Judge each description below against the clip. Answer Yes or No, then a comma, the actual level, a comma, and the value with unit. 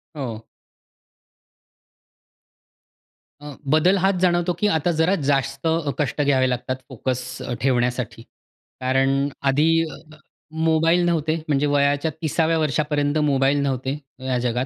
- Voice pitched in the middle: Yes, medium, 145 Hz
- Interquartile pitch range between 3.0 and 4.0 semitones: Yes, average, 3.5 semitones